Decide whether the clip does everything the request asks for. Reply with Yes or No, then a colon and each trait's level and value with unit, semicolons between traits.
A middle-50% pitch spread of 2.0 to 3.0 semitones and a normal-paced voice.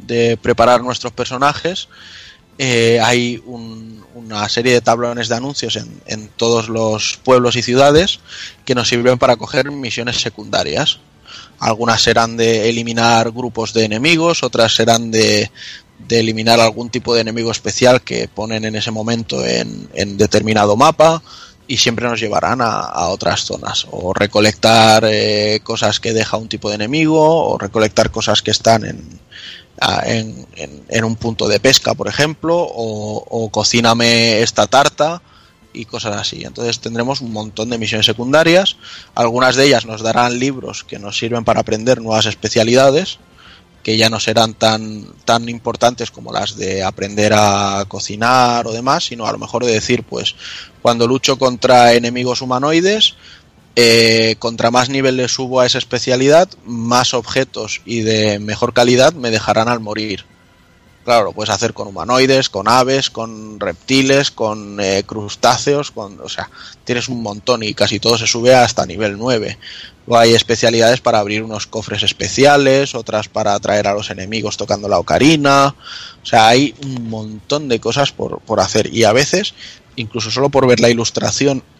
Yes: narrow, 2.5 semitones; average, 165 wpm